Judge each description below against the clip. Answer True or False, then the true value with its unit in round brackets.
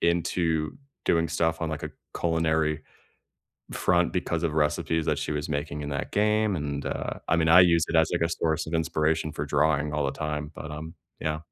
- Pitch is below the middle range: True (80 Hz)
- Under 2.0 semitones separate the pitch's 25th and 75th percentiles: True (1.6 semitones)